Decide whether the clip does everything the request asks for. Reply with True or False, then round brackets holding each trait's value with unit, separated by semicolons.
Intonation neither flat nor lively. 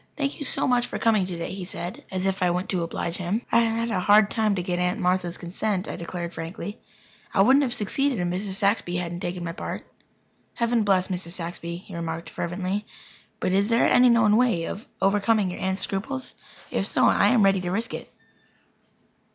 True (3.9 semitones)